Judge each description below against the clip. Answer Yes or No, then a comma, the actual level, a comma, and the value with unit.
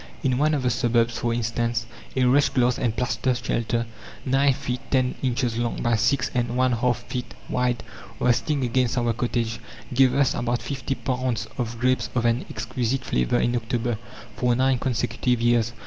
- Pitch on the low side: Yes, low, 120 Hz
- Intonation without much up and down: Yes, narrow, 1.5 semitones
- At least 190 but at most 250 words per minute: No, average, 175 wpm